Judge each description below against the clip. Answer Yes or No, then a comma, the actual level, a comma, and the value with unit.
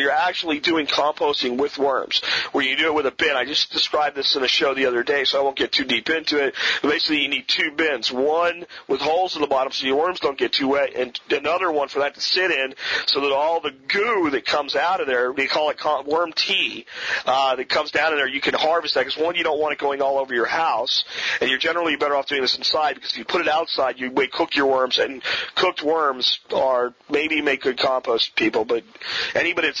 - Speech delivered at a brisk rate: Yes, fast, 250 wpm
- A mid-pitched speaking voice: Yes, medium, 145 Hz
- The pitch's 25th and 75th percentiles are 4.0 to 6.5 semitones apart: No, average, 3.4 semitones